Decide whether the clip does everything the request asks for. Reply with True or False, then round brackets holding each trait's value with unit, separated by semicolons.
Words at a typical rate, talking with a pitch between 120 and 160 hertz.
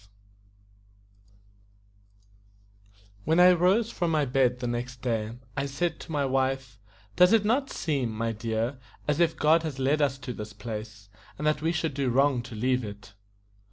True (165 wpm; 135 Hz)